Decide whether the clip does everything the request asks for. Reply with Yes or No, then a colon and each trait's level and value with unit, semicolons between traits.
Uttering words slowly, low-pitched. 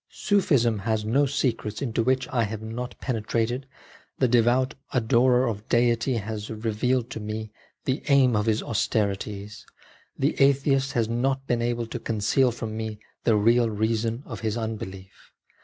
No: average, 155 wpm; low, 115 Hz